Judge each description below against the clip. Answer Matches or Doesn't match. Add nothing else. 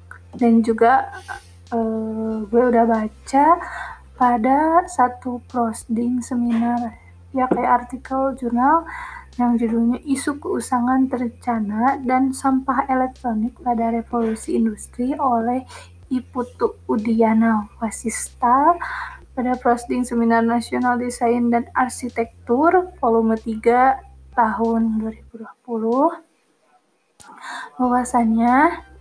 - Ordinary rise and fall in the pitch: Doesn't match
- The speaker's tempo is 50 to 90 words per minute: Matches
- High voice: Matches